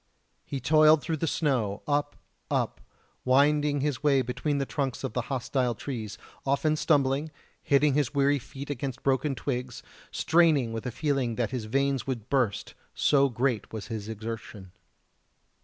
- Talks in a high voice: No, low, 135 Hz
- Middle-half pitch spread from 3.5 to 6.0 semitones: No, average, 3.0 semitones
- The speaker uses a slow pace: No, average, 155 wpm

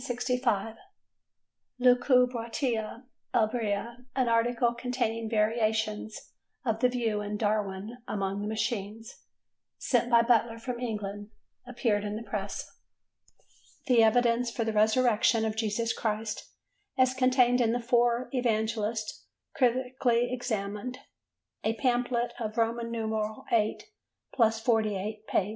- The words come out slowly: Yes, slow, 105 wpm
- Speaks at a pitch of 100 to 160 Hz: No, high, 230 Hz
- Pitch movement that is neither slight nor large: No, narrow, 2.2 semitones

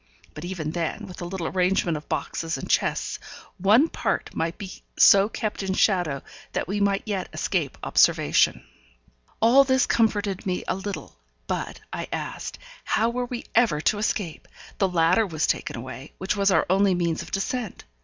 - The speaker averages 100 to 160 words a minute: No, average, 175 wpm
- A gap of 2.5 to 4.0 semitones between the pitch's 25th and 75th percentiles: Yes, average, 3.5 semitones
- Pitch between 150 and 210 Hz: Yes, high, 190 Hz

